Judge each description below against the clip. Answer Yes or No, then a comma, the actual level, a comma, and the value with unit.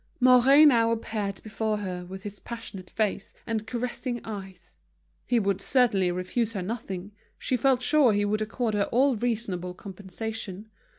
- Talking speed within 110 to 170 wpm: Yes, average, 155 wpm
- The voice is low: No, high, 215 Hz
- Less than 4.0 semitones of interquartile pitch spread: Yes, average, 3.5 semitones